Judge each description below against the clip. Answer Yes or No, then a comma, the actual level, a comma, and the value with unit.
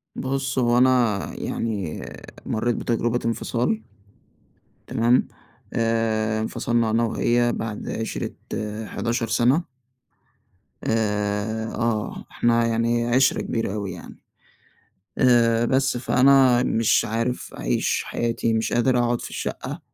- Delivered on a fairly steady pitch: Yes, narrow, 1.5 semitones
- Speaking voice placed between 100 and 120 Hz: Yes, low, 115 Hz